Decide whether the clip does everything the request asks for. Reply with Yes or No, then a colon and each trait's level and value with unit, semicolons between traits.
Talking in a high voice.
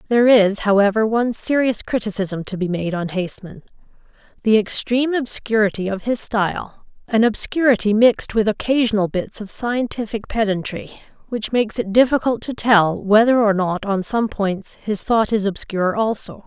Yes: high, 215 Hz